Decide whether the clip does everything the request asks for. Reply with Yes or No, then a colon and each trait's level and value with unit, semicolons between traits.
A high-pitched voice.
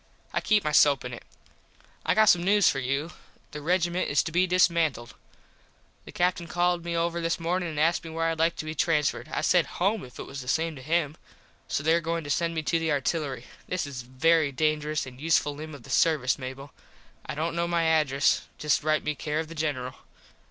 No: medium, 160 Hz